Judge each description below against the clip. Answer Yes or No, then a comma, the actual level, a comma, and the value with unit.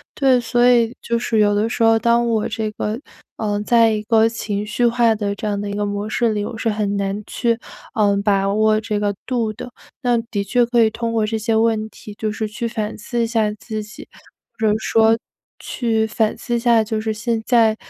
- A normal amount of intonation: No, narrow, 1.7 semitones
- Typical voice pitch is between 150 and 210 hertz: No, high, 220 Hz